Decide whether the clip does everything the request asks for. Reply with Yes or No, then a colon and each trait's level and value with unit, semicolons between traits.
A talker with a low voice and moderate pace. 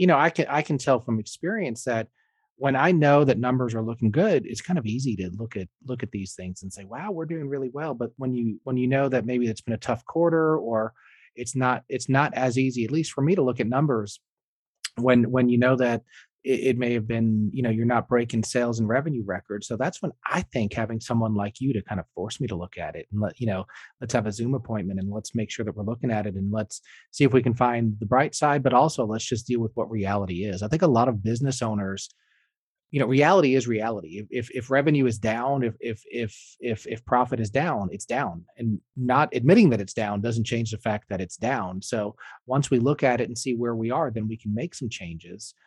No: low, 120 Hz; fast, 255 wpm